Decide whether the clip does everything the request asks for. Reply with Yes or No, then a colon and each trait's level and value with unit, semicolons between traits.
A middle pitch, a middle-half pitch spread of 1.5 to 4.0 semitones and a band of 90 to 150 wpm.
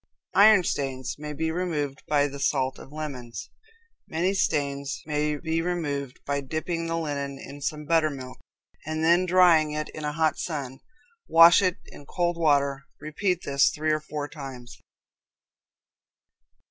Yes: medium, 150 Hz; average, 2.9 semitones; average, 145 wpm